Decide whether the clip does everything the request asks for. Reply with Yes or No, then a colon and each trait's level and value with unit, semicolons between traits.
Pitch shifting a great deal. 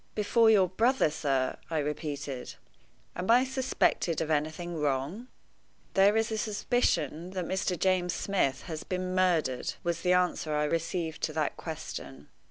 No: average, 4.2 semitones